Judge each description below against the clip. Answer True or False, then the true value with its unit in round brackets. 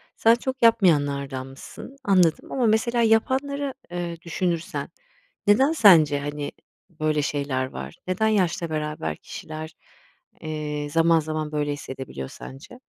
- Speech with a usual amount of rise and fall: False (6.9 semitones)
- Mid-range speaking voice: True (160 Hz)